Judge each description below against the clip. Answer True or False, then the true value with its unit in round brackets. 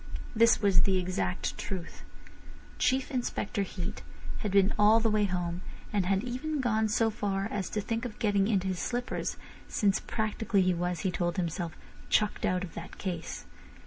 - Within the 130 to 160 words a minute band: False (175 wpm)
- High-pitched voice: True (200 Hz)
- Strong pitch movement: False (3.2 semitones)